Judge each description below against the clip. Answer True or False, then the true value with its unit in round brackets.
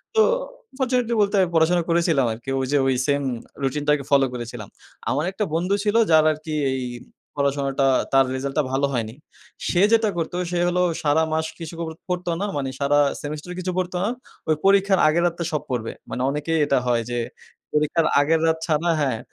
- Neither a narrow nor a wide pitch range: True (4.1 semitones)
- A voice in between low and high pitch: True (155 Hz)